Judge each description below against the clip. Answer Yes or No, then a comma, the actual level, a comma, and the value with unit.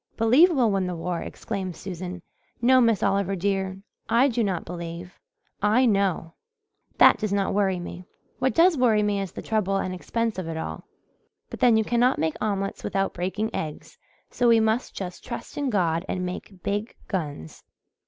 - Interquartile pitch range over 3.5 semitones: Yes, average, 4.0 semitones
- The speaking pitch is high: Yes, high, 195 Hz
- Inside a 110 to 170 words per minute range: No, average, 180 wpm